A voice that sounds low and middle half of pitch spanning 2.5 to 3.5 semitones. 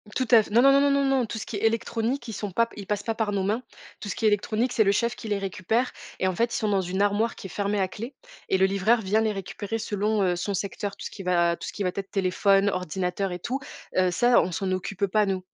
No: high, 205 Hz; average, 2.9 semitones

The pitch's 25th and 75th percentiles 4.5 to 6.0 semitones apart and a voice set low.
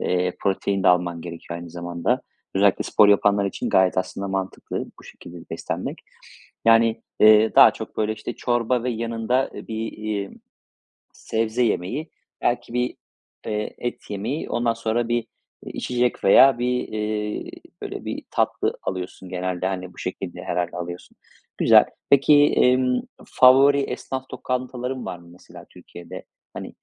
Yes: average, 4.9 semitones; low, 110 Hz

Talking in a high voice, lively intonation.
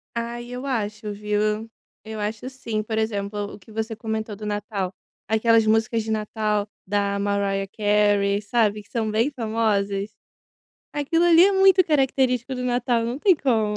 No: high, 220 Hz; average, 2.7 semitones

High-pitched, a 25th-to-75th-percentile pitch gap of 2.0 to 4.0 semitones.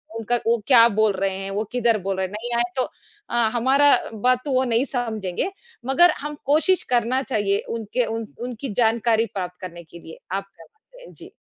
No: high, 230 Hz; average, 4.4 semitones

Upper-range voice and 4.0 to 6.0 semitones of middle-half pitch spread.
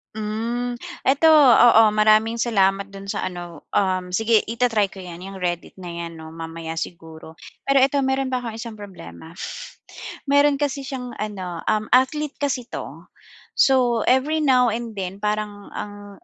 Yes: high, 215 Hz; average, 5.2 semitones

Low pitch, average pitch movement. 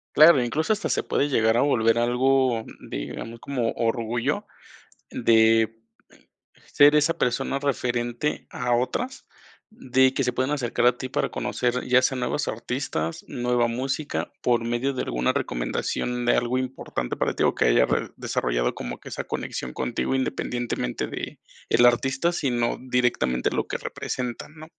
No: low, 125 Hz; narrow, 2.3 semitones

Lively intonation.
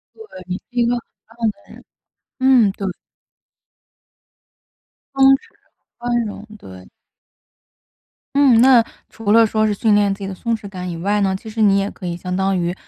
No: average, 3.5 semitones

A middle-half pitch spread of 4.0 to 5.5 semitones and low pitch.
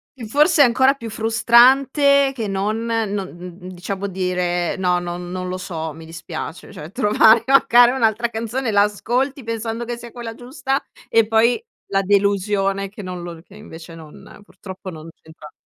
No: average, 4.6 semitones; high, 210 Hz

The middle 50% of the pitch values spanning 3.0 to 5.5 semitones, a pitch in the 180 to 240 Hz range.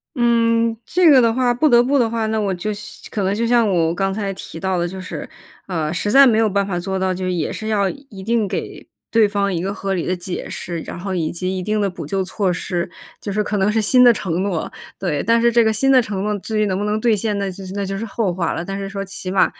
Yes: average, 3.3 semitones; high, 200 Hz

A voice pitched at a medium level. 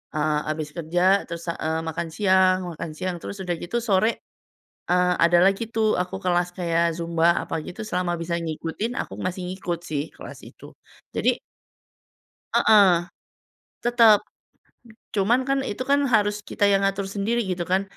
Yes: medium, 180 Hz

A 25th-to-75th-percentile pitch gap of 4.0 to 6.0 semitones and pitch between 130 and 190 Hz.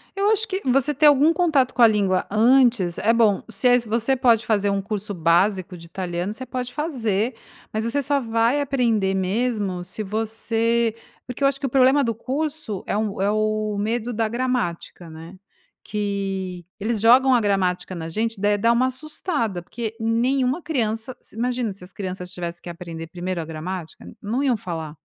No: average, 4.7 semitones; high, 220 Hz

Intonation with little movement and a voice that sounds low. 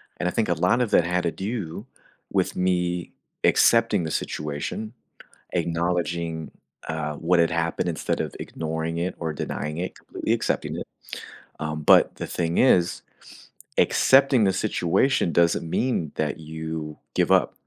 Yes: narrow, 2.3 semitones; very low, 85 Hz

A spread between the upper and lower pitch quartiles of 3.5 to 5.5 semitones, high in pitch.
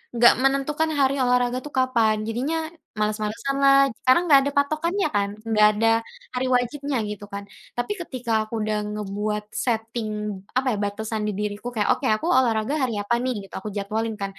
Yes: average, 4.1 semitones; high, 235 Hz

